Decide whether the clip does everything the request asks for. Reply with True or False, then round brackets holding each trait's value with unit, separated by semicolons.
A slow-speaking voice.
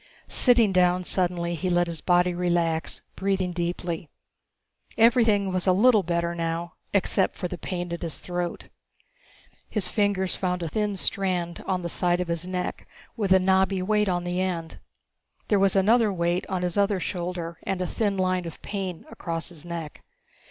False (175 wpm)